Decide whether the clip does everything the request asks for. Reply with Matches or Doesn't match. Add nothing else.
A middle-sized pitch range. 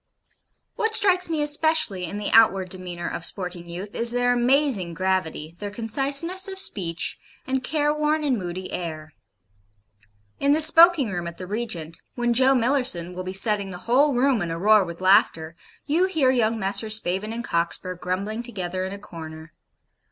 Doesn't match